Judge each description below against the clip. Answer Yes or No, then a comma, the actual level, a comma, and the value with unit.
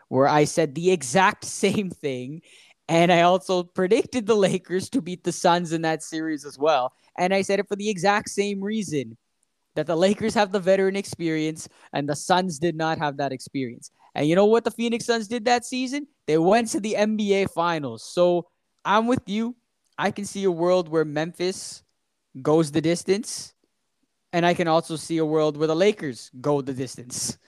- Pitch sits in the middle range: Yes, medium, 175 Hz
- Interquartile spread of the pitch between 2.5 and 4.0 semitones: No, average, 4.5 semitones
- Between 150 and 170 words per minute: No, average, 195 wpm